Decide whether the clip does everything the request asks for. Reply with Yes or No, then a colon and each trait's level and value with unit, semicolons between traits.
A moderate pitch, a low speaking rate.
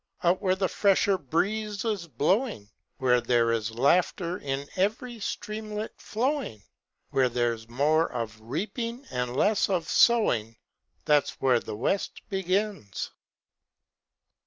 Yes: medium, 170 Hz; slow, 120 wpm